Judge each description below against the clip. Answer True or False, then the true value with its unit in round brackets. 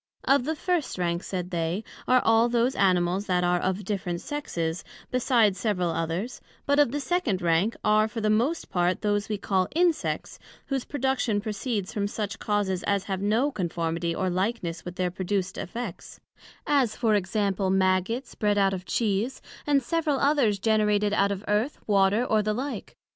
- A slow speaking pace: False (175 wpm)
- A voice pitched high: True (205 Hz)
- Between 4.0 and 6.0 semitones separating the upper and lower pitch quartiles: True (4.4 semitones)